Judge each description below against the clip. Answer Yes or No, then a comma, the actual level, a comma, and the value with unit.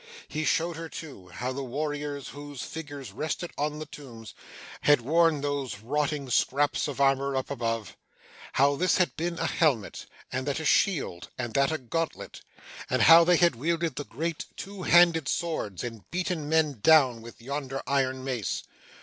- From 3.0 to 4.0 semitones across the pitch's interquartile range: Yes, average, 3.7 semitones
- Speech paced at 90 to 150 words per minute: No, average, 170 wpm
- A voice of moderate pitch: Yes, medium, 145 Hz